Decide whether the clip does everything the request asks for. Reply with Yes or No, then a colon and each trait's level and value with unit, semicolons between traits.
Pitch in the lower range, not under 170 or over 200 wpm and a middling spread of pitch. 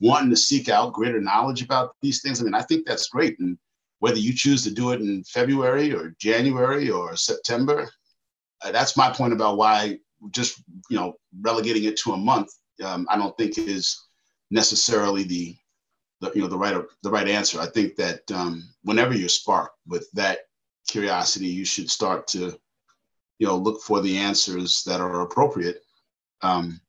No: low, 110 Hz; average, 180 wpm; wide, 6.6 semitones